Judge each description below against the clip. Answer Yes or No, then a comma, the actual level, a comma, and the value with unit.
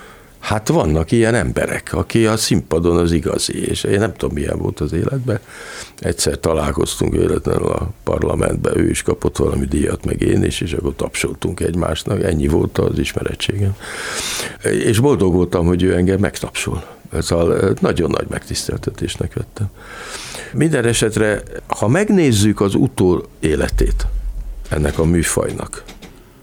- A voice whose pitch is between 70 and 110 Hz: Yes, very low, 95 Hz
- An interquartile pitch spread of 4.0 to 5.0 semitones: Yes, average, 4.5 semitones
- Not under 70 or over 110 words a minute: No, average, 140 wpm